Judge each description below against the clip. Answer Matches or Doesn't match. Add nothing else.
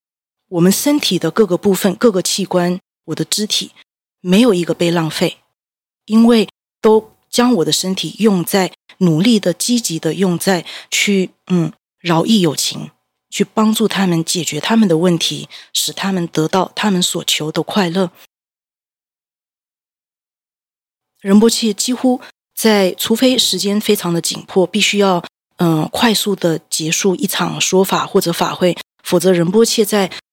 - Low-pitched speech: Doesn't match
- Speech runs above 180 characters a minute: Matches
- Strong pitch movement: Doesn't match